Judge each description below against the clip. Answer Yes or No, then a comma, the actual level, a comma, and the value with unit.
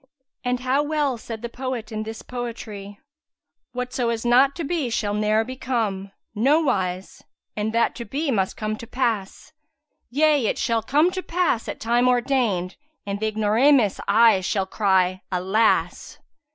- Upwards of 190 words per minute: No, average, 165 wpm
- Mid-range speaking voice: No, high, 230 Hz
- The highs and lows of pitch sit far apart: No, average, 3.7 semitones